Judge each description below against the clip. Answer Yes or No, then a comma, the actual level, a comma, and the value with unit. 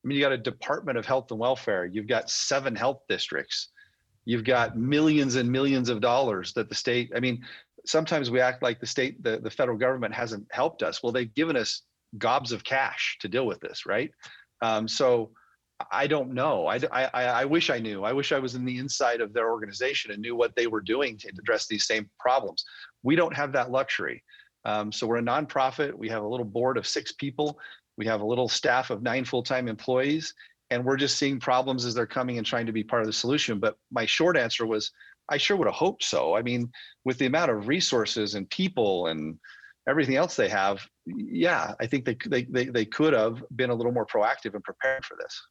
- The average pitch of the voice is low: Yes, low, 125 Hz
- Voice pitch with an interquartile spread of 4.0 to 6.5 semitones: No, average, 2.8 semitones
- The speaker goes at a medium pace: No, fast, 225 wpm